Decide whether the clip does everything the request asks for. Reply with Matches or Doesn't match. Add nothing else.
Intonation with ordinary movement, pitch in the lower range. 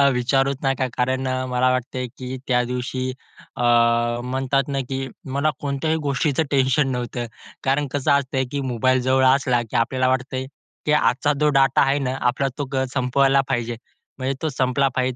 Doesn't match